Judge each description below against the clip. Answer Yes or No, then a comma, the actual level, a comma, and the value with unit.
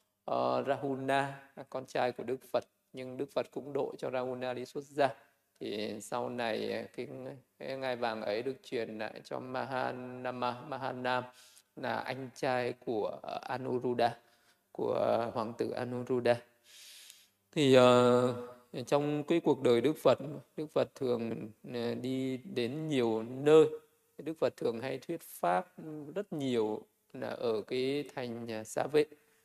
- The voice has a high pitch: No, low, 125 Hz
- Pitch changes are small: Yes, narrow, 2.3 semitones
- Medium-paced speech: No, slow, 145 wpm